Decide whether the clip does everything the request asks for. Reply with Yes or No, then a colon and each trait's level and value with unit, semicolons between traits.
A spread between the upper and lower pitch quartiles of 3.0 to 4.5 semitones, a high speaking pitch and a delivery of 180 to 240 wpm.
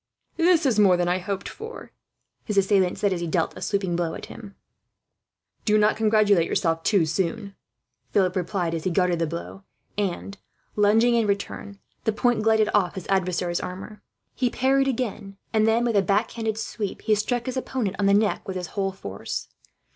Yes: average, 3.3 semitones; high, 200 Hz; average, 190 wpm